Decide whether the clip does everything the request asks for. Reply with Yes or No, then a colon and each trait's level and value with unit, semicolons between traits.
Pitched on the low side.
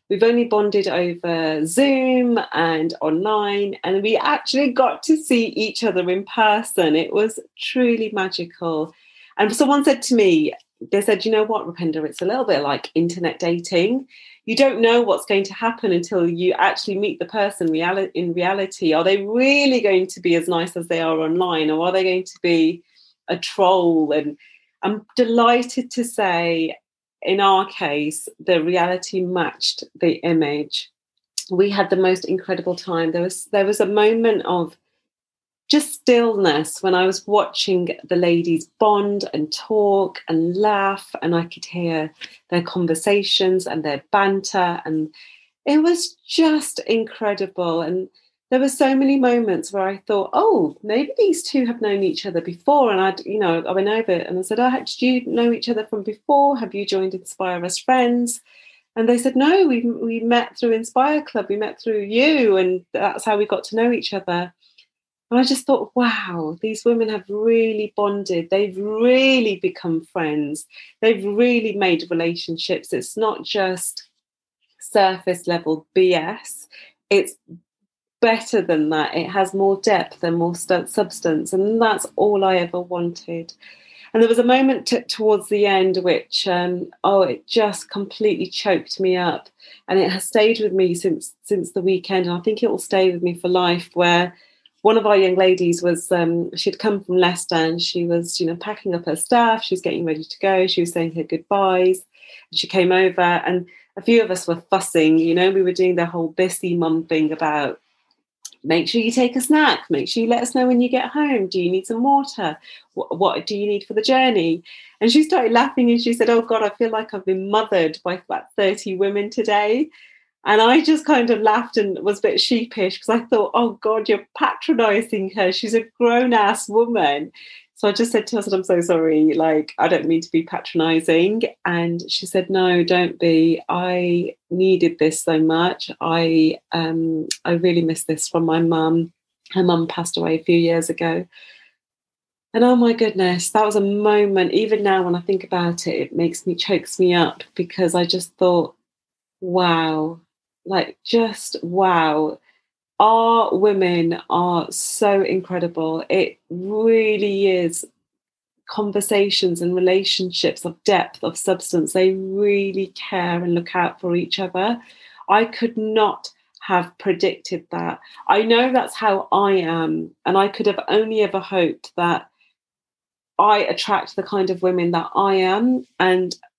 No: high, 190 Hz